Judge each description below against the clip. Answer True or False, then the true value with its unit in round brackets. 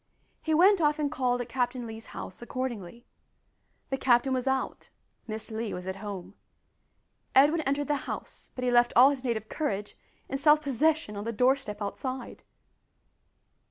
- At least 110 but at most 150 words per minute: False (160 wpm)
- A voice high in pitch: True (250 Hz)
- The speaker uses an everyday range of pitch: True (4.1 semitones)